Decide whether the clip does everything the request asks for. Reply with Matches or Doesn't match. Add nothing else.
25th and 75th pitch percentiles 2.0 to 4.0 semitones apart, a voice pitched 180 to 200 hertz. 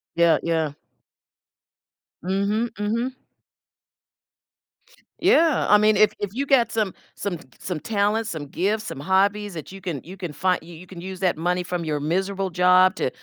Matches